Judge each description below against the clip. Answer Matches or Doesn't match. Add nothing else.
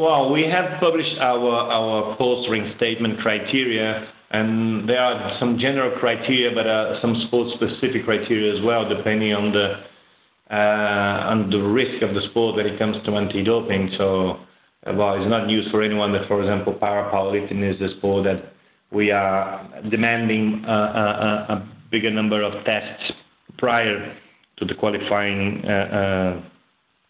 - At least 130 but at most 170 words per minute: Matches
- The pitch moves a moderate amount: Doesn't match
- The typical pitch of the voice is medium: Doesn't match